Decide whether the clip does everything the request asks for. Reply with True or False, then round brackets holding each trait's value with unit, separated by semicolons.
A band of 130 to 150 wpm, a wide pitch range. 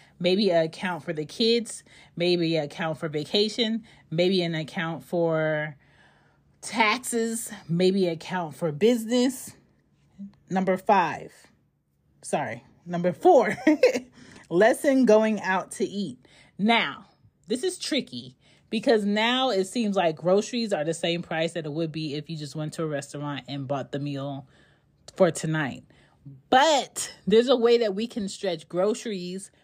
True (145 wpm; 5.7 semitones)